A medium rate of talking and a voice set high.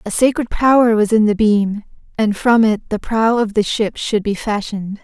No: fast, 215 wpm; high, 215 Hz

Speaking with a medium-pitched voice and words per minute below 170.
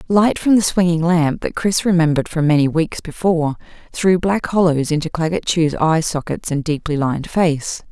No: medium, 165 Hz; average, 180 wpm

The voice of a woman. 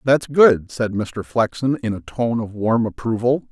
No: male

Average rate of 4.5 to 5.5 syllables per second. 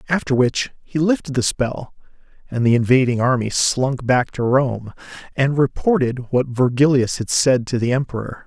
Yes: 4.7 syllables/s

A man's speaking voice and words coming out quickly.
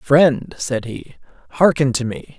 No: male; average, 150 wpm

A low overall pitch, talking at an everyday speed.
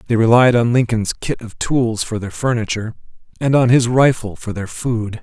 Yes: low, 115 Hz; average, 195 wpm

